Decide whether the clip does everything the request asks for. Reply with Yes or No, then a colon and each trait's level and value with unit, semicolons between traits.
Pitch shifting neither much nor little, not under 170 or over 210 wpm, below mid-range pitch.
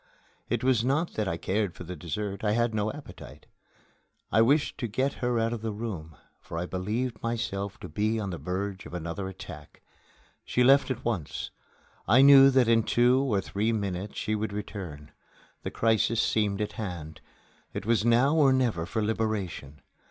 Yes: average, 3.8 semitones; average, 180 wpm; low, 110 Hz